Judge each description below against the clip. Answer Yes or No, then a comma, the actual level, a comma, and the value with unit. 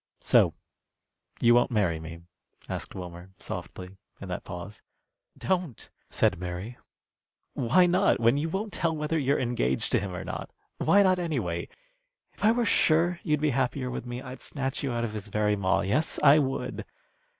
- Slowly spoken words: No, average, 170 wpm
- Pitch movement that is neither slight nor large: No, wide, 7.7 semitones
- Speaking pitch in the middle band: No, low, 125 Hz